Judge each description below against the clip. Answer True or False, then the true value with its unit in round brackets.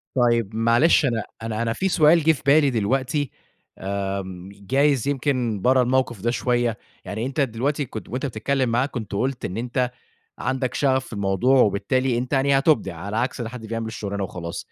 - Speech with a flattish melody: False (3.5 semitones)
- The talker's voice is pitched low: True (125 Hz)